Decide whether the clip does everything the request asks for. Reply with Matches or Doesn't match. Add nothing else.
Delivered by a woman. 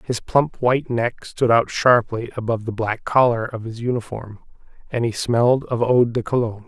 Doesn't match